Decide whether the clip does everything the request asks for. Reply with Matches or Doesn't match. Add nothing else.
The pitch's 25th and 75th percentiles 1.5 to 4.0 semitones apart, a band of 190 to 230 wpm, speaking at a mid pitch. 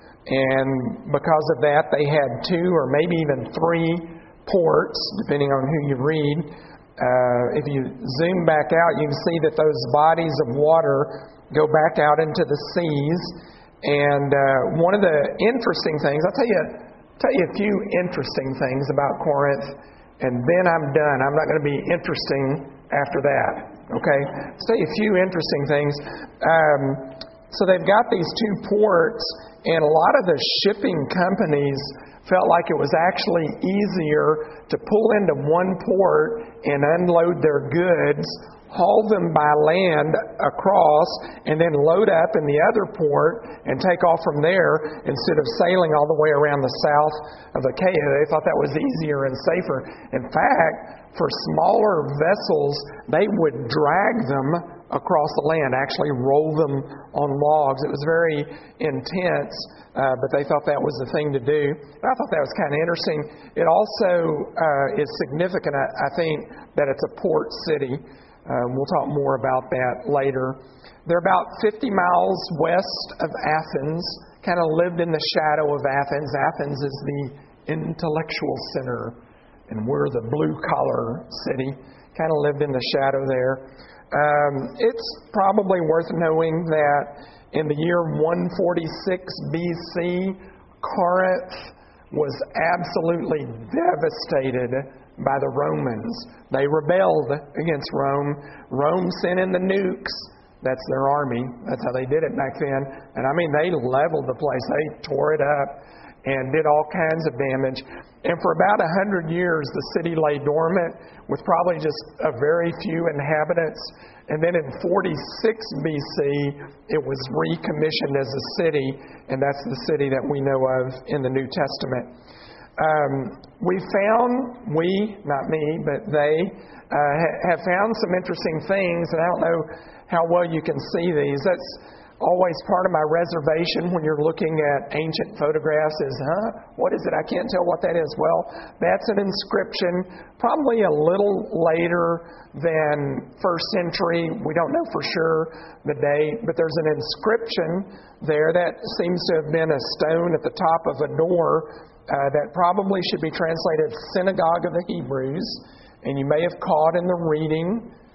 Doesn't match